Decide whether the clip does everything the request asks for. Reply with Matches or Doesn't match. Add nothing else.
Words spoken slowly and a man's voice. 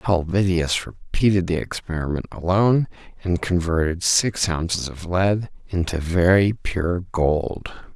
Matches